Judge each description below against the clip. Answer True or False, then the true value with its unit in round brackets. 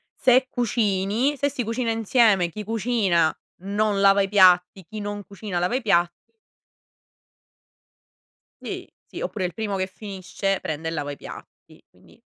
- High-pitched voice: True (200 Hz)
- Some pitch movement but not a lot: True (3.3 semitones)